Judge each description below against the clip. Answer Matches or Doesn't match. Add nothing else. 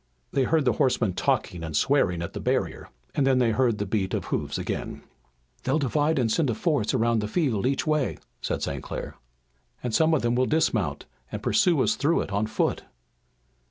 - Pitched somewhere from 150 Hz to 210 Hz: Doesn't match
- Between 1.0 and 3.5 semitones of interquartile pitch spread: Doesn't match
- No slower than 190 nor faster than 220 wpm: Matches